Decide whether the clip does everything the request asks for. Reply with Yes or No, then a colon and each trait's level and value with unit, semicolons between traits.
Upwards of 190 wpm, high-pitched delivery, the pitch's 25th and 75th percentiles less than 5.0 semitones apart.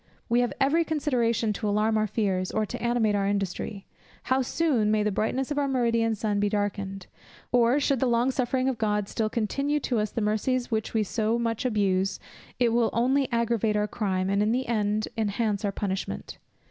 Yes: average, 200 wpm; high, 220 Hz; average, 2.8 semitones